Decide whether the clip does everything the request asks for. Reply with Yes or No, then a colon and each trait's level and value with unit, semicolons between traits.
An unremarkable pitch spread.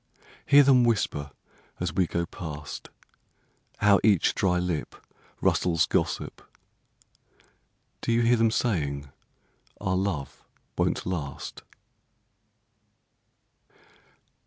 No: wide, 6.3 semitones